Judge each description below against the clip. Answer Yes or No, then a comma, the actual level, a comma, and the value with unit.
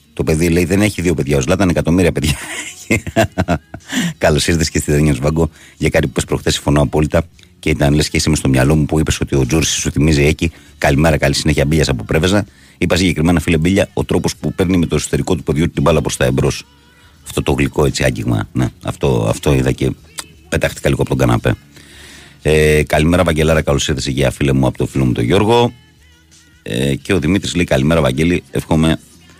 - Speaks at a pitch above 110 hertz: No, very low, 80 Hz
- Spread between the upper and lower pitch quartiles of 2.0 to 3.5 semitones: Yes, average, 3.0 semitones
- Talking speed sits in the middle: No, fast, 205 wpm